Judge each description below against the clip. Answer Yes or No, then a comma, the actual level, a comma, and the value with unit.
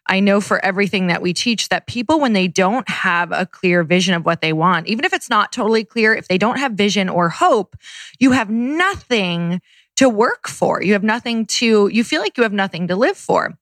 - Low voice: No, high, 205 Hz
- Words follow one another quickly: Yes, fast, 230 wpm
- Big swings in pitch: No, average, 4.4 semitones